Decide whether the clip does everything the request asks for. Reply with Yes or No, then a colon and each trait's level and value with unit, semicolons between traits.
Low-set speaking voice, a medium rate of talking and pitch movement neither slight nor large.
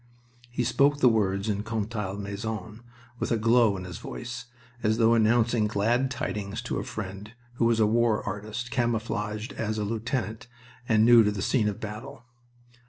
No: low, 110 Hz; average, 170 wpm; narrow, 2.0 semitones